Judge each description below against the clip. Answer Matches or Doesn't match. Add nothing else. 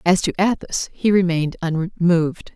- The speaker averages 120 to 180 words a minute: Matches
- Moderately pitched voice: Matches